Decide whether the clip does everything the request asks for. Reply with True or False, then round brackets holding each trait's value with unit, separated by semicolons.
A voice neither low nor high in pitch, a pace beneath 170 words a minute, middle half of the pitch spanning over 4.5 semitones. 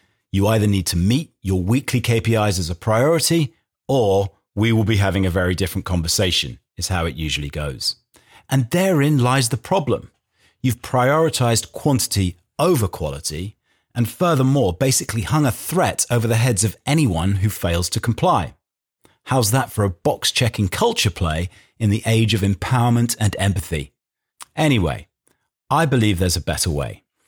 False (110 Hz; 155 wpm; 5.1 semitones)